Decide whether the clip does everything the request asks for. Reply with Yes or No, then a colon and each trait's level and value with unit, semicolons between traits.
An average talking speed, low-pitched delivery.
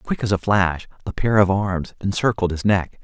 No: fast, 215 wpm; very low, 95 Hz